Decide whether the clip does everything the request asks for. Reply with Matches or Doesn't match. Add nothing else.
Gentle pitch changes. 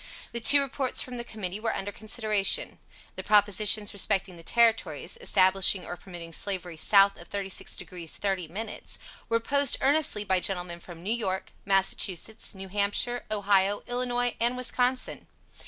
Doesn't match